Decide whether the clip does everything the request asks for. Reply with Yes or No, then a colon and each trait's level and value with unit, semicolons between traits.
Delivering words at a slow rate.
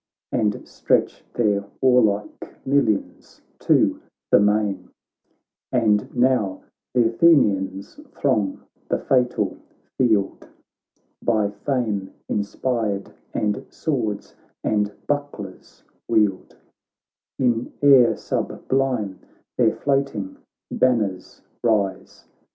Yes: slow, 85 wpm